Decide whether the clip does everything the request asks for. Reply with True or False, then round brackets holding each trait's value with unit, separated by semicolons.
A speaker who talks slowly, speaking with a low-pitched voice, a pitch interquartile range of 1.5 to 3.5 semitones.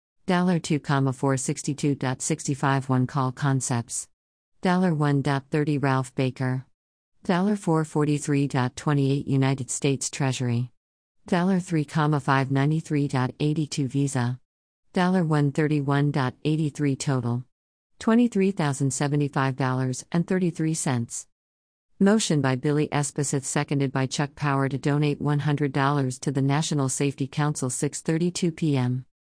False (70 wpm; 145 Hz; 2.6 semitones)